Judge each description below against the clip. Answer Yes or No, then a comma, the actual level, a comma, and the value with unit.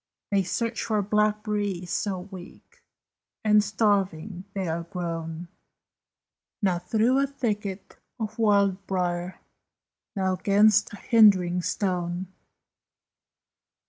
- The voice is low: No, high, 195 Hz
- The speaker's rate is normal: No, slow, 100 wpm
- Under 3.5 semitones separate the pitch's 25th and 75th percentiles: Yes, average, 2.8 semitones